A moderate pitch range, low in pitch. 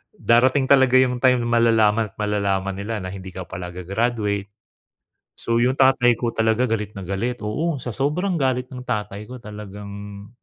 Yes: average, 3.7 semitones; low, 115 Hz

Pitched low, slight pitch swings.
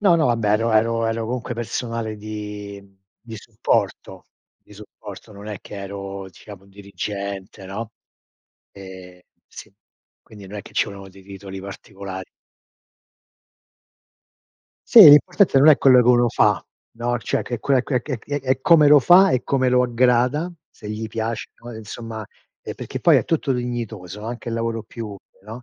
No: low, 115 Hz; average, 3.6 semitones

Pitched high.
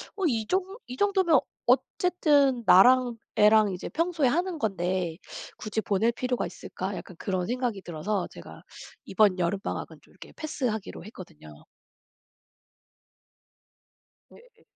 Yes: high, 220 Hz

